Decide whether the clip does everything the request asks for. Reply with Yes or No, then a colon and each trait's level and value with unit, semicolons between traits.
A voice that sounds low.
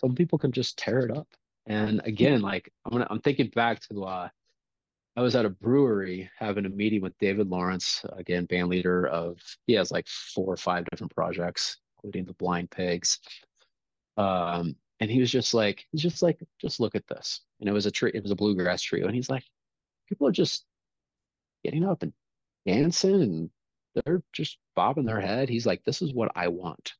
Yes: low, 105 Hz